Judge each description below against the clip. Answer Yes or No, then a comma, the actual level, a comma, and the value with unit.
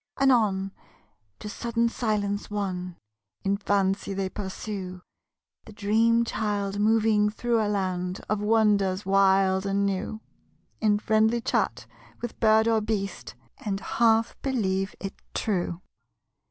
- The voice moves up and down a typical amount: No, narrow, 2.2 semitones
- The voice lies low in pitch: No, high, 205 Hz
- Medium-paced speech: No, slow, 120 wpm